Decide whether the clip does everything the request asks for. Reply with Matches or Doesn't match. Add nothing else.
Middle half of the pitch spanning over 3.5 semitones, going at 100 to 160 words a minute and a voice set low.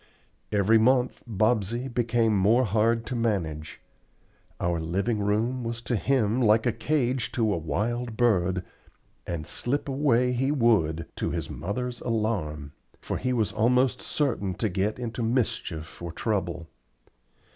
Matches